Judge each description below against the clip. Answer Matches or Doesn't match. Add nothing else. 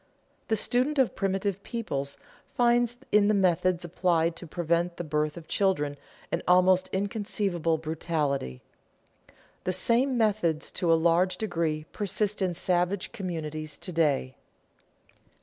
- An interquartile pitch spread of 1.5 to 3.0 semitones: Doesn't match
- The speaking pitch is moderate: Matches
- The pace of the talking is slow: Matches